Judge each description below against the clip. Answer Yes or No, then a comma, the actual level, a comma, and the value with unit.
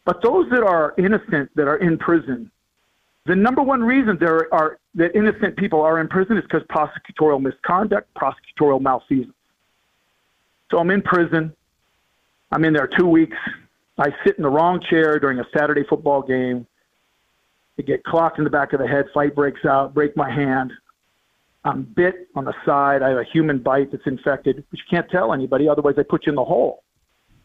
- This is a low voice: No, medium, 155 Hz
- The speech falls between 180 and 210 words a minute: Yes, average, 190 wpm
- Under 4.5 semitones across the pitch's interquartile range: Yes, average, 3.7 semitones